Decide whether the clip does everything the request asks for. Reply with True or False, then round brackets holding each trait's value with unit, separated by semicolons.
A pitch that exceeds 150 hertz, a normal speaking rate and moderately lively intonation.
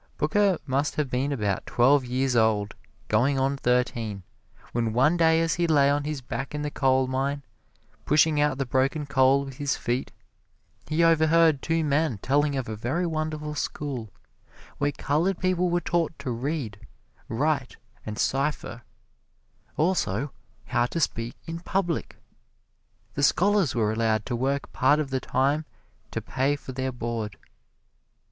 False (140 Hz; 155 wpm; 3.7 semitones)